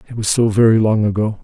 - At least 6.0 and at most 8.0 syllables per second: Yes, 6.5 syllables/s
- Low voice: Yes, low, 110 Hz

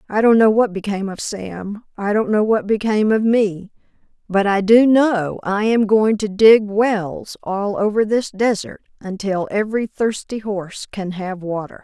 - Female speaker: Yes, female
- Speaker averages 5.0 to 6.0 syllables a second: No, 4.5 syllables/s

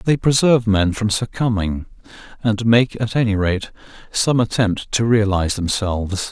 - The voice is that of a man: Yes, male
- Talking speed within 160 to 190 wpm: No, average, 145 wpm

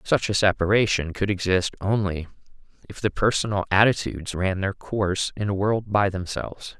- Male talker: Yes, male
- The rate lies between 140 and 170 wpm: Yes, average, 160 wpm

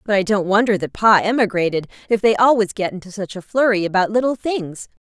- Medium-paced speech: No, fast, 210 wpm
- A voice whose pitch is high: Yes, high, 205 Hz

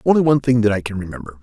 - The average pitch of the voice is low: Yes, low, 110 Hz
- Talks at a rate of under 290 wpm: No, fast, 295 wpm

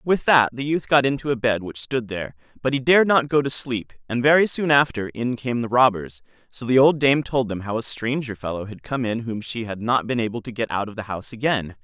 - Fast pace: Yes, fast, 265 wpm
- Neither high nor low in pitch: No, low, 120 Hz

